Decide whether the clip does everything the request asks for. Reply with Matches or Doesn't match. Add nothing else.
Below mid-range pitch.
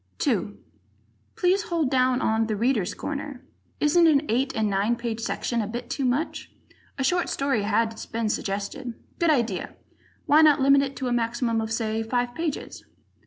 Doesn't match